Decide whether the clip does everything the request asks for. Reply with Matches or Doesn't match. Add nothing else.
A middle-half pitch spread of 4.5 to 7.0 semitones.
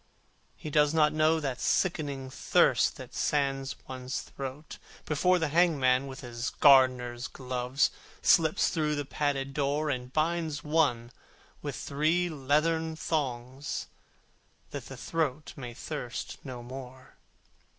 Doesn't match